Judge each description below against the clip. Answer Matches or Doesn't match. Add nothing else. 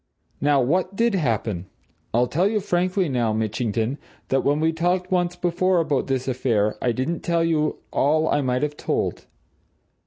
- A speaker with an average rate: Matches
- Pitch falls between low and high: Matches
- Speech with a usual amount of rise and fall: Doesn't match